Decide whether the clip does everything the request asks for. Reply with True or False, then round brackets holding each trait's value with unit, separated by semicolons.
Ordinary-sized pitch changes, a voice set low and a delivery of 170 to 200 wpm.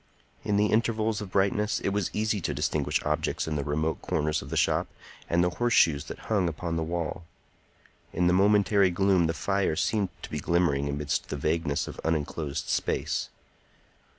True (4.6 semitones; 85 Hz; 175 wpm)